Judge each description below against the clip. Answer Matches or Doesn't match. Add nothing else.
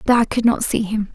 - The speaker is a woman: Matches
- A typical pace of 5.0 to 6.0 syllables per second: Matches